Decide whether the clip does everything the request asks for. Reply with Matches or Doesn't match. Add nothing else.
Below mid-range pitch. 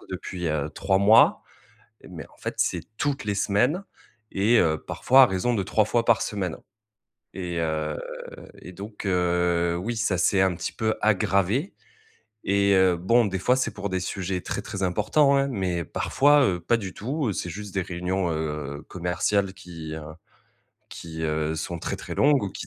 Matches